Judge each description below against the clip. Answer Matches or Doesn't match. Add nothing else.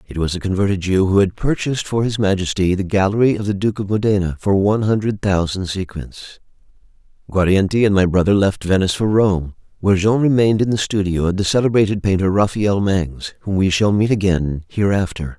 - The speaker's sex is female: Doesn't match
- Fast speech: Doesn't match